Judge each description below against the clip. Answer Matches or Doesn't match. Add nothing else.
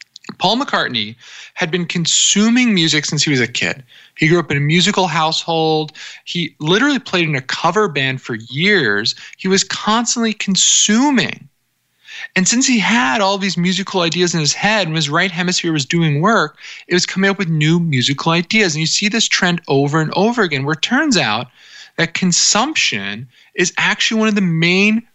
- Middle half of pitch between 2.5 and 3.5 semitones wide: Doesn't match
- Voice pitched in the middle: Matches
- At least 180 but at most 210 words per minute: Matches